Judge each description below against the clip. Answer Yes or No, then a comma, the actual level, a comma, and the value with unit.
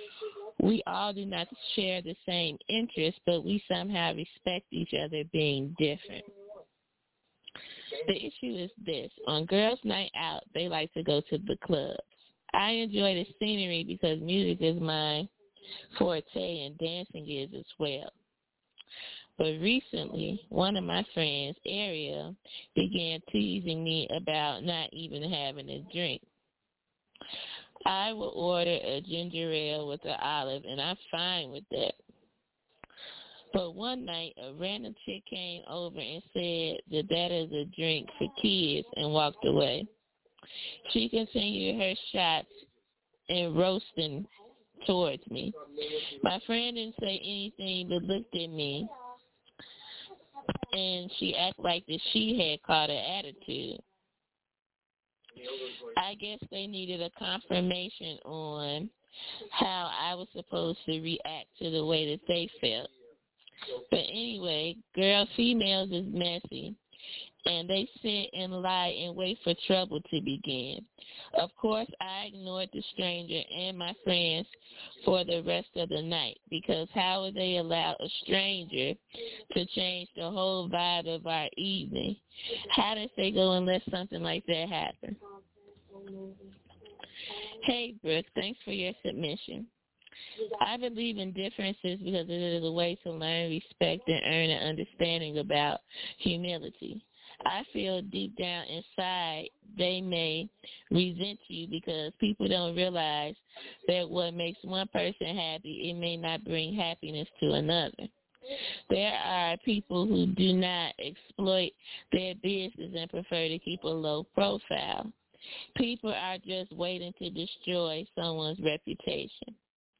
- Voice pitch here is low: No, medium, 180 Hz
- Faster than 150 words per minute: No, slow, 135 wpm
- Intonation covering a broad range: No, average, 3.9 semitones